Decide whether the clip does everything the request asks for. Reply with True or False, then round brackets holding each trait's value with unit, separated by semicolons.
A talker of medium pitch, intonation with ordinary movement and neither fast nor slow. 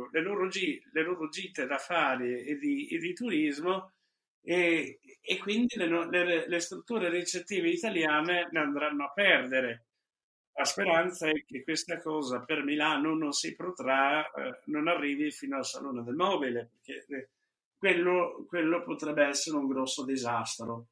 True (160 Hz; 4.2 semitones; 145 wpm)